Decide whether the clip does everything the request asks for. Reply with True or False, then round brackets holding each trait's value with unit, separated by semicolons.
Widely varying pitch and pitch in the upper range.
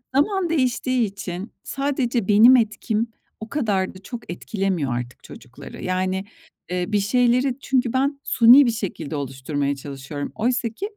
True (5.8 semitones; 220 Hz)